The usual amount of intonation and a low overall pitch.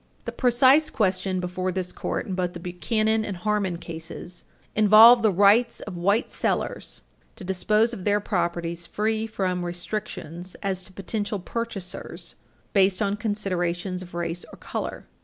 No: average, 3.3 semitones; high, 195 Hz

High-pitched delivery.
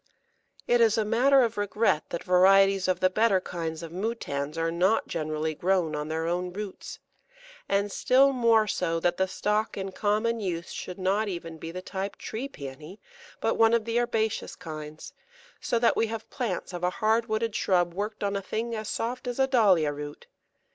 Yes: high, 195 Hz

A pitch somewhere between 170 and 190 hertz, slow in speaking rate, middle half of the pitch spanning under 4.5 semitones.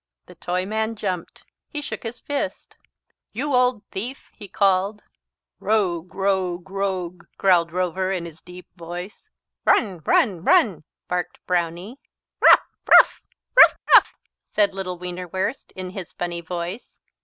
Yes: medium, 185 Hz; slow, 130 wpm; average, 2.9 semitones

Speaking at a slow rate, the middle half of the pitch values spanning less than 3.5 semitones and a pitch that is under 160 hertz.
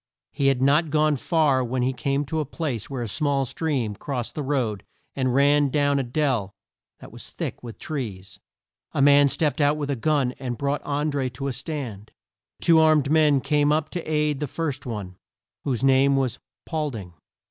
No: average, 200 wpm; average, 2.9 semitones; medium, 140 Hz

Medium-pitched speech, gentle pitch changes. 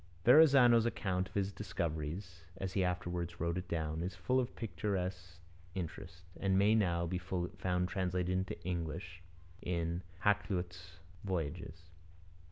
No: very low, 90 Hz; narrow, 2.2 semitones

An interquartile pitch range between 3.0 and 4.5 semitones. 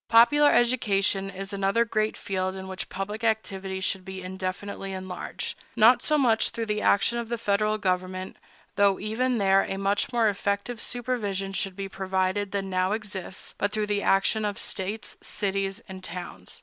No: narrow, 2.4 semitones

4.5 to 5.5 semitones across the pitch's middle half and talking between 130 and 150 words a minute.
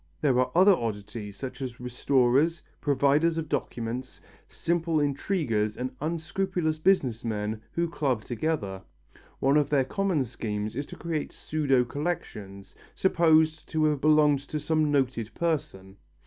Yes: average, 5.1 semitones; slow, 135 wpm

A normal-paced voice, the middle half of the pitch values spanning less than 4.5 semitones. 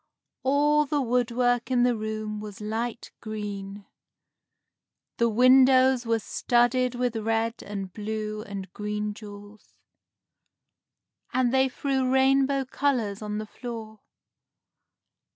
No: slow, 110 wpm; average, 3.3 semitones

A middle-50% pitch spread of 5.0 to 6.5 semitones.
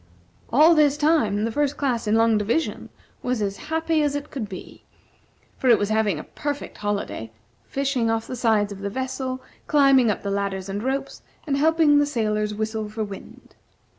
Yes: average, 5.3 semitones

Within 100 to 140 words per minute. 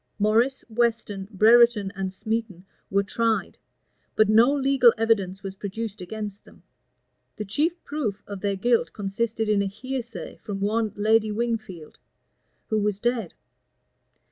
Yes: slow, 135 wpm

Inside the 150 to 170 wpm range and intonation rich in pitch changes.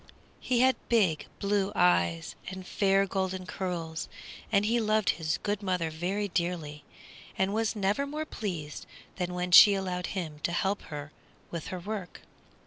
No: average, 155 wpm; average, 3.3 semitones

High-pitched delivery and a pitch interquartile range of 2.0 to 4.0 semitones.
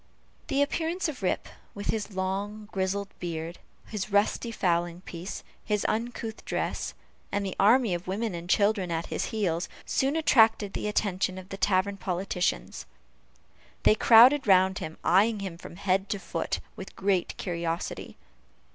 Yes: high, 195 Hz; average, 3.0 semitones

